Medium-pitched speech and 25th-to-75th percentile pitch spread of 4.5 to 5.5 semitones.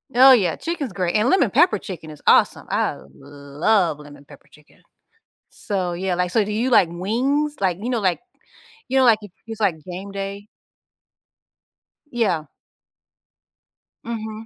No: high, 200 Hz; average, 4.9 semitones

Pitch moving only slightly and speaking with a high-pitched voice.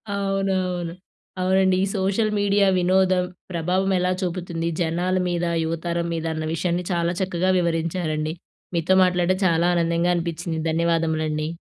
No: narrow, 2.0 semitones; medium, 175 Hz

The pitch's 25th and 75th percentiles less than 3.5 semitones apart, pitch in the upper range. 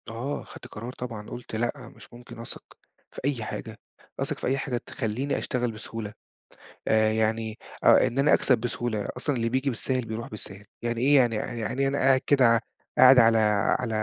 No: narrow, 2.5 semitones; low, 120 Hz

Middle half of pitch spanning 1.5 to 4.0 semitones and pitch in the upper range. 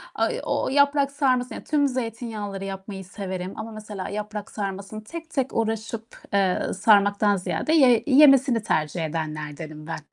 No: average, 4.9 semitones; high, 210 Hz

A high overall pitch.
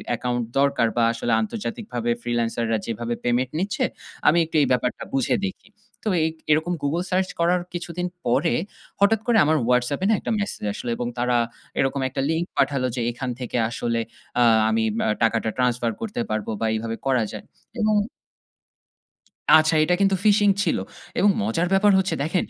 No: low, 135 Hz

